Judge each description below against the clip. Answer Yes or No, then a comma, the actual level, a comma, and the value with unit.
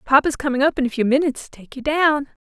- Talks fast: Yes, fast, 290 wpm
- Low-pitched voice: No, very high, 275 Hz